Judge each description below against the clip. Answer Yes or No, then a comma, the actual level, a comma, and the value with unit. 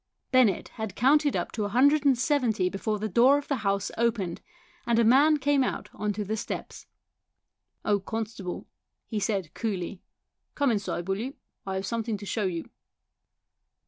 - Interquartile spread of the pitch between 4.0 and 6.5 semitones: Yes, average, 4.5 semitones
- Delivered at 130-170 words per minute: No, average, 180 wpm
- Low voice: No, high, 220 Hz